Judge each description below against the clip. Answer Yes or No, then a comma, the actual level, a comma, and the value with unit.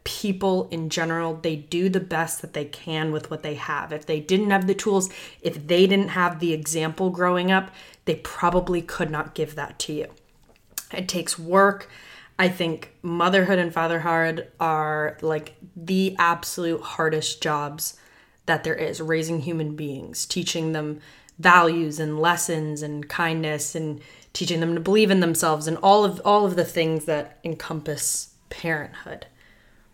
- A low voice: No, medium, 165 Hz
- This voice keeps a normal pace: Yes, average, 160 wpm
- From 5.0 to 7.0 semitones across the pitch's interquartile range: No, narrow, 2.4 semitones